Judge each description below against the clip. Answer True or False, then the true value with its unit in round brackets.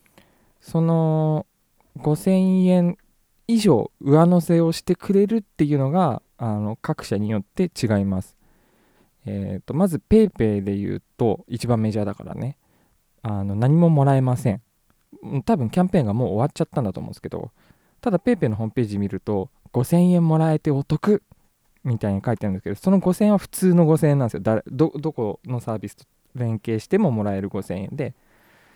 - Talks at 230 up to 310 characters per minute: False (345 characters per minute)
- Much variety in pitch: True (8.2 semitones)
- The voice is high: False (140 Hz)